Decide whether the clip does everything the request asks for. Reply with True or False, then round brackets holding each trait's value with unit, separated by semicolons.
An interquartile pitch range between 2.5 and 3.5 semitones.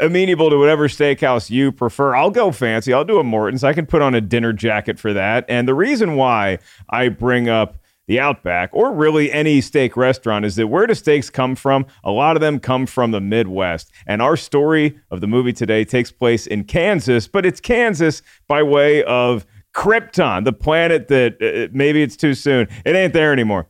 False (4.6 semitones)